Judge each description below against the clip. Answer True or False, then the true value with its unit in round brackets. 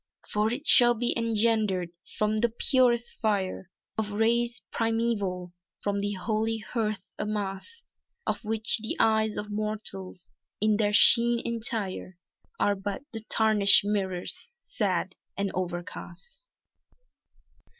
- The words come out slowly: True (120 wpm)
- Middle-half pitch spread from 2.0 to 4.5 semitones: True (2.4 semitones)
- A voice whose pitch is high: True (215 Hz)